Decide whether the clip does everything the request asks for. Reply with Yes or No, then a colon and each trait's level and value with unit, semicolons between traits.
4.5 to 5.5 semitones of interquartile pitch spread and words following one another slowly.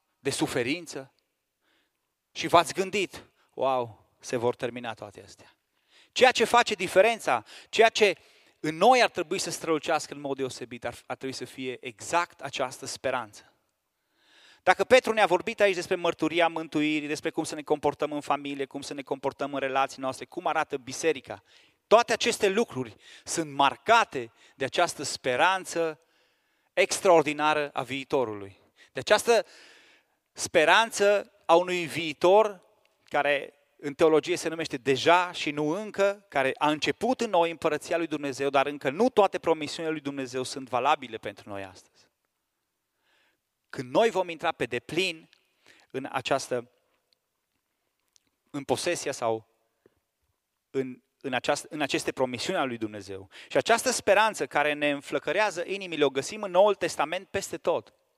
No: average, 5.2 semitones; average, 140 wpm